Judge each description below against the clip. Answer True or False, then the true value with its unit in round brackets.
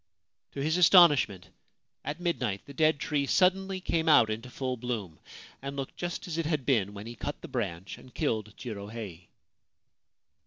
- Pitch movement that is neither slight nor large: False (6.7 semitones)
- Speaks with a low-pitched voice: True (130 Hz)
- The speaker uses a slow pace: False (165 wpm)